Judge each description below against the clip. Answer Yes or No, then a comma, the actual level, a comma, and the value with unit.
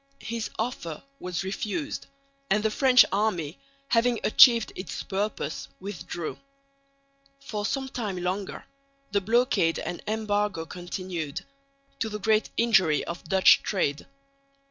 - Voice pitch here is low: No, high, 205 Hz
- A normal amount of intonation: Yes, average, 3.7 semitones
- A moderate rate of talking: No, slow, 120 wpm